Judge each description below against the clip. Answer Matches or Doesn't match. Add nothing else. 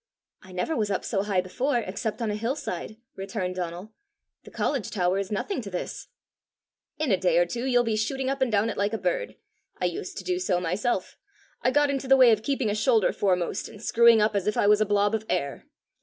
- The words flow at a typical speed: Doesn't match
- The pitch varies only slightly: Doesn't match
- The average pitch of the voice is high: Matches